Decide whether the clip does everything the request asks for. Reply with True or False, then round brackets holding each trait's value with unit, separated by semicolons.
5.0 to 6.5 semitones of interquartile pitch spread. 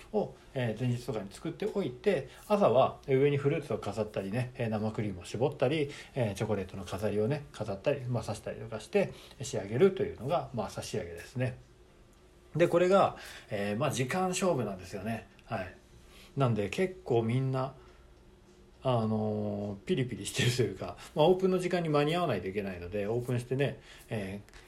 True (5.6 semitones)